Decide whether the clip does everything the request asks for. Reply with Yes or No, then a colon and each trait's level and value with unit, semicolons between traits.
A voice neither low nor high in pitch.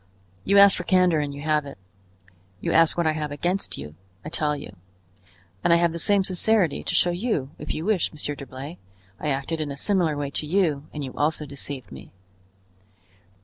Yes: medium, 155 Hz